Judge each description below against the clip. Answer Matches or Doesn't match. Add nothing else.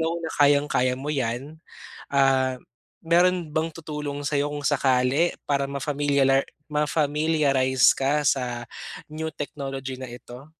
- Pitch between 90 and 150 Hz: Matches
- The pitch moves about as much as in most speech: Doesn't match